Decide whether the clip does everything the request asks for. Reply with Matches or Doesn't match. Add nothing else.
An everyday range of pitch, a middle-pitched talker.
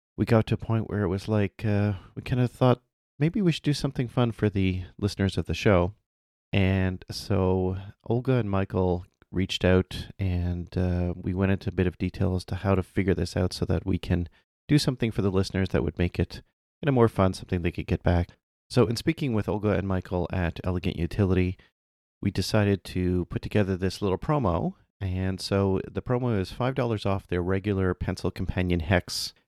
Doesn't match